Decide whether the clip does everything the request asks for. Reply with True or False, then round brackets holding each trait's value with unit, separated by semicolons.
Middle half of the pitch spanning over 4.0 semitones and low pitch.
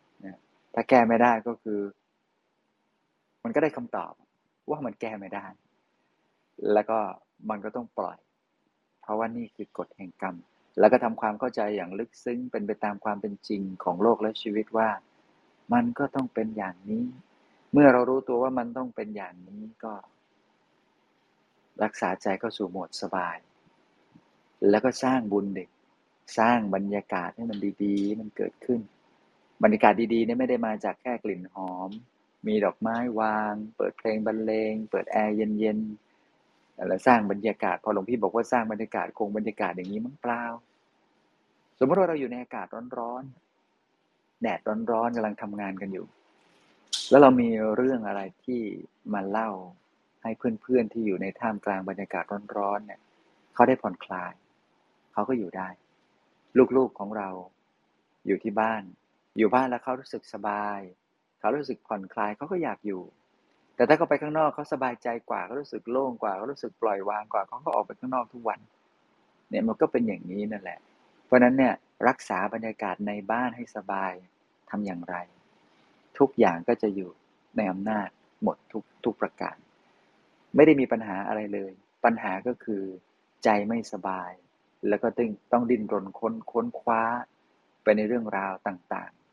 False (3.2 semitones; 110 Hz)